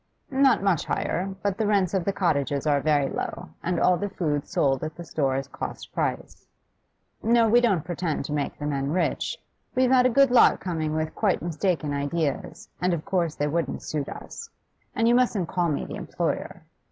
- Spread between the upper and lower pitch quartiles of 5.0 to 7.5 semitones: Yes, average, 5.3 semitones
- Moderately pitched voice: Yes, medium, 170 Hz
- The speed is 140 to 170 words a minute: No, average, 200 wpm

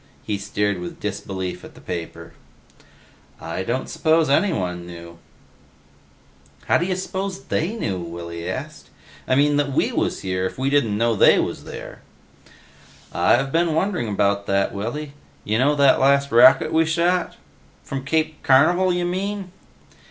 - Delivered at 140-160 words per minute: Yes, average, 150 wpm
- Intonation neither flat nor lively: No, wide, 8.6 semitones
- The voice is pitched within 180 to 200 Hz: No, low, 135 Hz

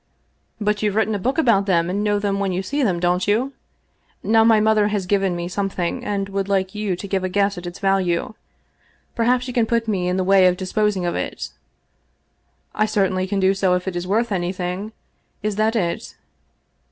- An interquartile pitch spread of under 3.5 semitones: Yes, narrow, 2.5 semitones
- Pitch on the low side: No, high, 195 Hz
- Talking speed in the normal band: No, fast, 215 wpm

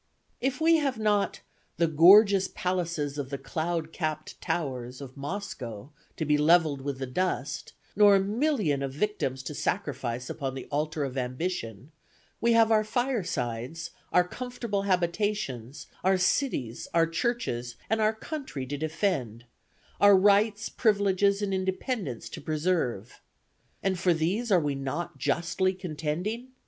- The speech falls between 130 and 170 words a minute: Yes, average, 140 wpm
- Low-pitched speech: No, medium, 170 Hz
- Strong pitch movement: Yes, wide, 6.6 semitones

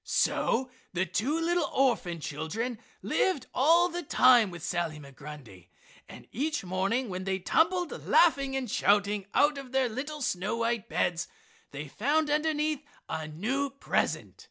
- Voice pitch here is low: No, high, 240 Hz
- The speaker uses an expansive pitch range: Yes, wide, 8.5 semitones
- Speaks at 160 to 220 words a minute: No, average, 145 wpm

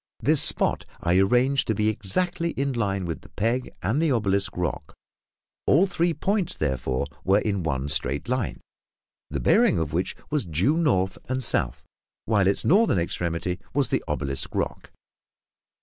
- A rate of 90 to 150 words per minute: No, average, 160 wpm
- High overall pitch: No, low, 105 Hz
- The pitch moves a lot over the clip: Yes, wide, 7.9 semitones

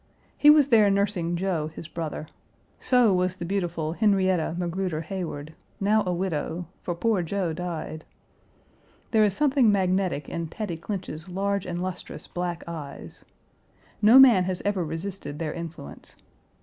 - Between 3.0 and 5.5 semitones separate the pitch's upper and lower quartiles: Yes, average, 3.3 semitones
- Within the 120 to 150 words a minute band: Yes, average, 145 wpm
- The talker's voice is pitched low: No, medium, 180 Hz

